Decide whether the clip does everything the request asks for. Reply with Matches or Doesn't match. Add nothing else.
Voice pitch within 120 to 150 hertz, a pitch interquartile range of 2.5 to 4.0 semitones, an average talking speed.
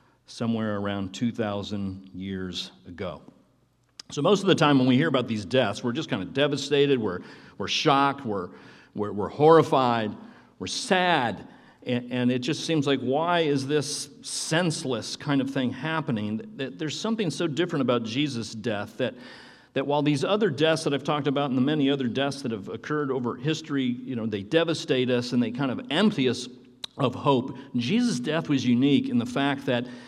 Matches